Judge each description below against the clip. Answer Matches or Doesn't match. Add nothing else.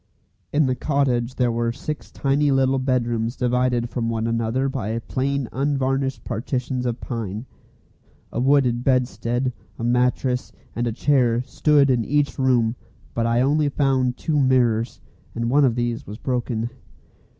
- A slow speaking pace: Doesn't match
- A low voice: Matches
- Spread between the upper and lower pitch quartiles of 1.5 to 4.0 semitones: Matches